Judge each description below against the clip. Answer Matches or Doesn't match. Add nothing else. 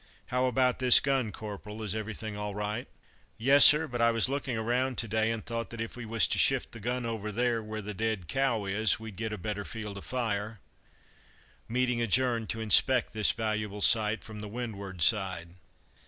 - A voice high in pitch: Doesn't match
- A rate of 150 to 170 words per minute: Doesn't match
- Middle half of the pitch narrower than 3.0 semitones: Matches